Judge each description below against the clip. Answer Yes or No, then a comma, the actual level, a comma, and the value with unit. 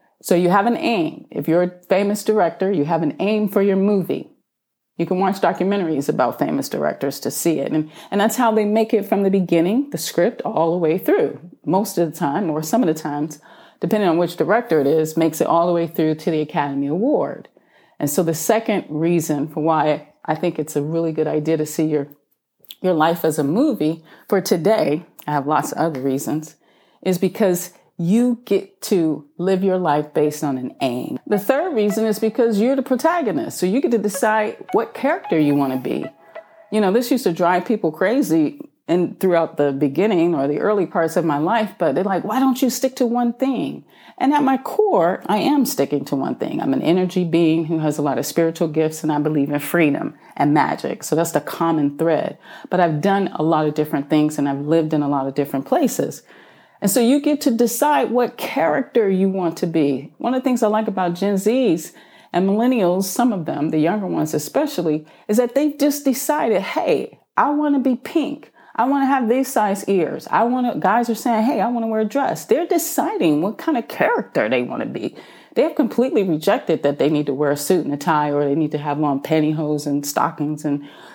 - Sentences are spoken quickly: Yes, fast, 225 wpm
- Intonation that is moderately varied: No, wide, 6.7 semitones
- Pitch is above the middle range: No, medium, 180 Hz